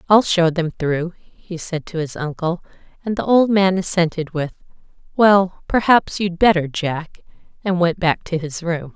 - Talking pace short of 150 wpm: No, average, 175 wpm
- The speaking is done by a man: No, female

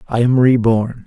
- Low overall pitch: Yes, low, 120 Hz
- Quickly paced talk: No, average, 170 wpm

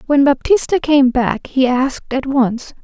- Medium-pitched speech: No, very high, 270 Hz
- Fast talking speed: No, average, 170 wpm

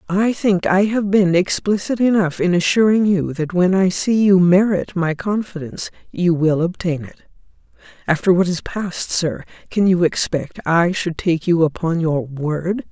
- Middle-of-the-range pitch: Yes, medium, 180 Hz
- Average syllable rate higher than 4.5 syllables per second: No, 4.4 syllables/s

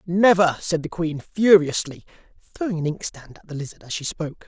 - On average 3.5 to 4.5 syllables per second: No, 5.5 syllables/s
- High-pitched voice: No, medium, 165 Hz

